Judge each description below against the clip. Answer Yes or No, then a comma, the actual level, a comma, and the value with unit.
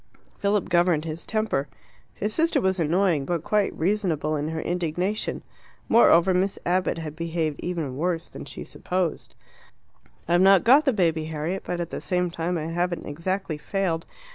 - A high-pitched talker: No, medium, 175 Hz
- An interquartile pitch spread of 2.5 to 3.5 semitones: Yes, average, 2.9 semitones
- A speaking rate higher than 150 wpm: Yes, average, 165 wpm